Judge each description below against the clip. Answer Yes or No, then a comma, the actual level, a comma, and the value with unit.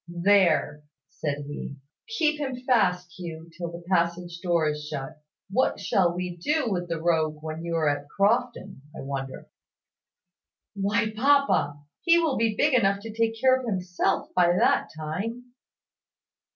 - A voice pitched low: No, medium, 180 Hz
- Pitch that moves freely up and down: Yes, wide, 6.0 semitones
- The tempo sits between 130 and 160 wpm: Yes, average, 150 wpm